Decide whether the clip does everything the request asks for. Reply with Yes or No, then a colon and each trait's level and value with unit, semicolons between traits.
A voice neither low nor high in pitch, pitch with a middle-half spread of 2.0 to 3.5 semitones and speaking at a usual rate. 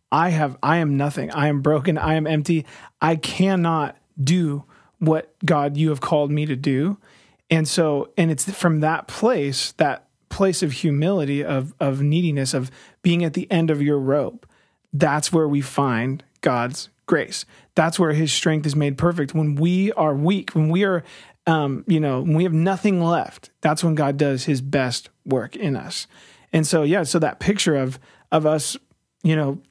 Yes: medium, 155 Hz; average, 2.9 semitones; average, 185 wpm